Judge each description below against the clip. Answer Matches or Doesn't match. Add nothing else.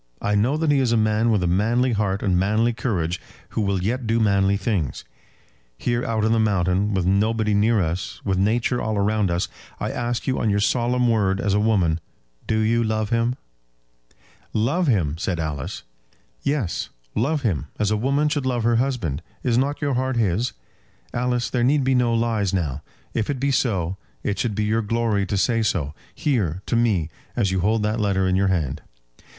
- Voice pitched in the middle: Doesn't match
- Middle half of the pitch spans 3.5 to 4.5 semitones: Matches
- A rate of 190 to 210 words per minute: Matches